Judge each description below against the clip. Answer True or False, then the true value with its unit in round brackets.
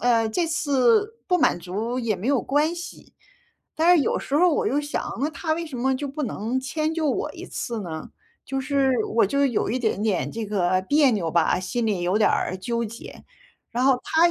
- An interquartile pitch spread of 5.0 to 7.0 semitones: True (5.5 semitones)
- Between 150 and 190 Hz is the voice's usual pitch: False (250 Hz)